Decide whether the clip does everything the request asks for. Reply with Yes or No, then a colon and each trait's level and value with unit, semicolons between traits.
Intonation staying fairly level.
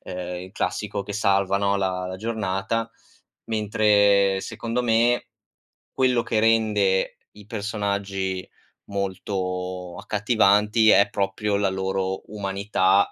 Yes: narrow, 2.1 semitones